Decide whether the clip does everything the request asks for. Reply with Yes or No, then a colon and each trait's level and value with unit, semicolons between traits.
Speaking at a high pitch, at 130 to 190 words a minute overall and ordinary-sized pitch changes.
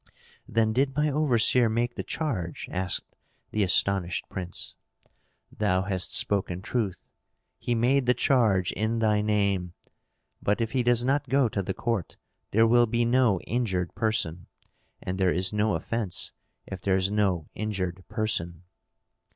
No: low, 105 Hz; average, 150 wpm; average, 4.2 semitones